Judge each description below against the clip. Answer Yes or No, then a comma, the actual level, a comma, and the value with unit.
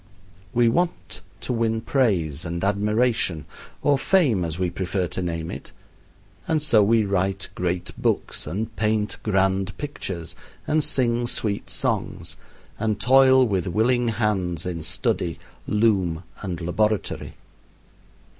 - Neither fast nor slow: No, slow, 125 wpm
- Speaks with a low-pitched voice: Yes, low, 105 Hz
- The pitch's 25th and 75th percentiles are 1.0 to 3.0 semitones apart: No, average, 4.6 semitones